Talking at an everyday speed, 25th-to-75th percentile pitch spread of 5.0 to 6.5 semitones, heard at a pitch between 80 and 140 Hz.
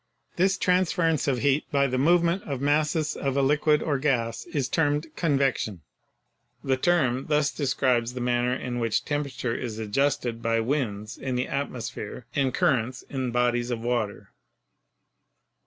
No: average, 155 wpm; average, 3.4 semitones; low, 135 Hz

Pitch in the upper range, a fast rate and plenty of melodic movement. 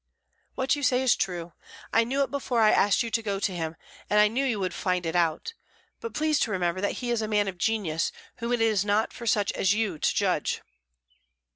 No: high, 210 Hz; fast, 235 wpm; average, 4.5 semitones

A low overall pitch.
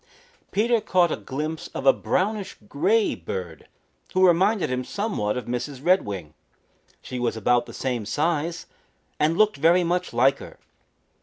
No: medium, 150 Hz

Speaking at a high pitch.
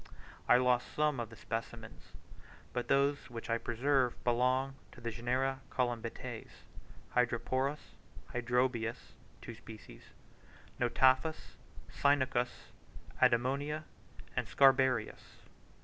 No: low, 125 Hz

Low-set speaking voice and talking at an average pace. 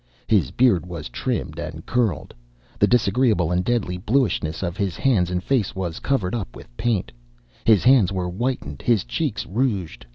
Yes: very low, 95 Hz; average, 165 wpm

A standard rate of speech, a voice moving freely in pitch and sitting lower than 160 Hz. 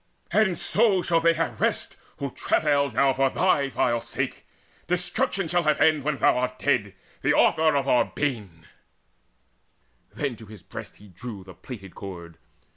Yes: average, 165 wpm; wide, 6.7 semitones; low, 135 Hz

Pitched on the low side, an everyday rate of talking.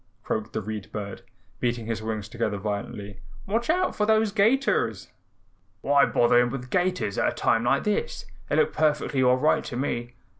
Yes: low, 120 Hz; average, 180 wpm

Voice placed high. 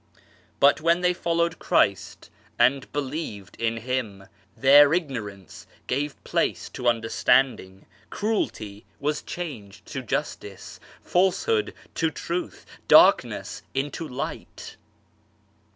No: medium, 140 Hz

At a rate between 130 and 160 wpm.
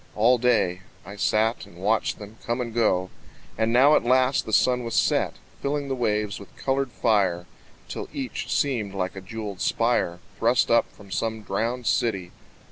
No: average, 175 wpm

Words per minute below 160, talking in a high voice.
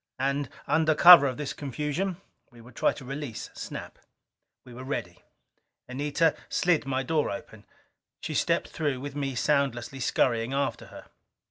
No: average, 150 wpm; medium, 140 Hz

